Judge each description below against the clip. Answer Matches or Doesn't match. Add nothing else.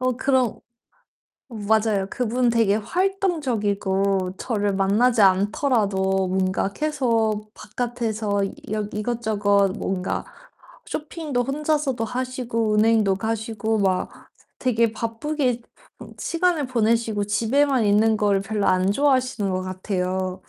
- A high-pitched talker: Matches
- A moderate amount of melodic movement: Matches